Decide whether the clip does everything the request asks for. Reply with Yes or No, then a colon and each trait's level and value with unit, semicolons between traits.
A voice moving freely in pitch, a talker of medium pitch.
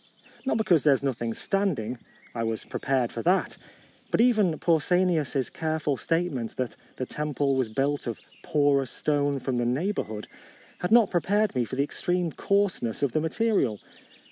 Yes: wide, 5.8 semitones; medium, 145 Hz